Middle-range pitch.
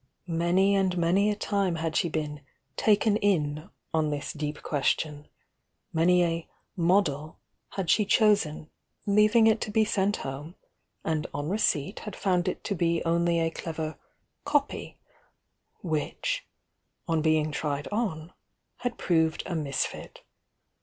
Yes: medium, 170 Hz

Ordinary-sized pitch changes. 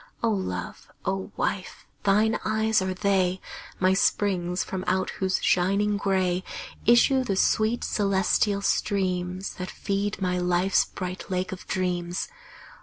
No: narrow, 1.9 semitones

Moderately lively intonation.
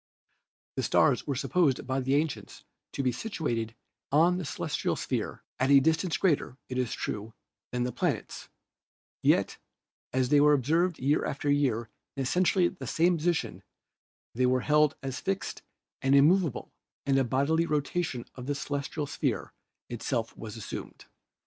Yes: average, 4.1 semitones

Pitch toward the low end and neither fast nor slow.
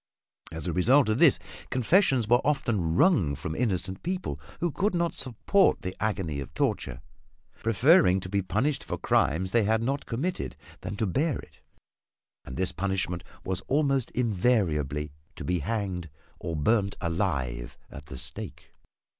Yes: low, 100 Hz; average, 155 wpm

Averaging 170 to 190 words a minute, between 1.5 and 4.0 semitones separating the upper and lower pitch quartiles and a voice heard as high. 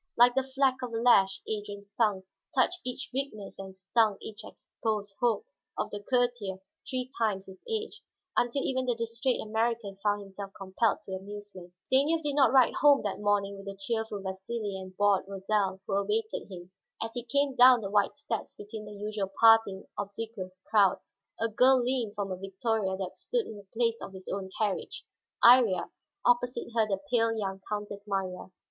Yes: average, 180 wpm; average, 3.7 semitones; high, 215 Hz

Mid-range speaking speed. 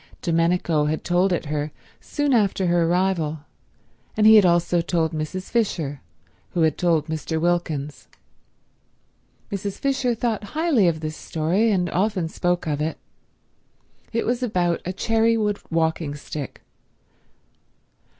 No: slow, 130 wpm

